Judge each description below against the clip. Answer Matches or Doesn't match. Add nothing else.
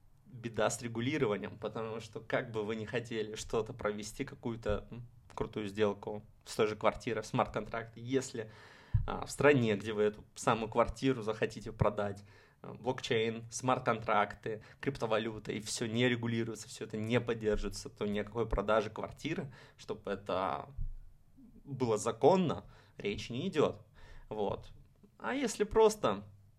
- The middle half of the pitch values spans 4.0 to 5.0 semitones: Doesn't match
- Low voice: Matches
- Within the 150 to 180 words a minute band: Doesn't match